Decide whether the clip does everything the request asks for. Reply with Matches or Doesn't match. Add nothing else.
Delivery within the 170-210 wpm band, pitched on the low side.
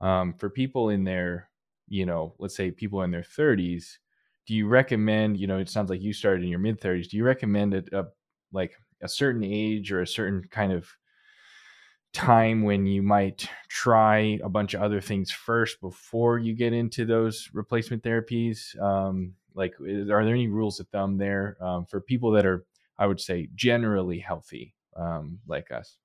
Matches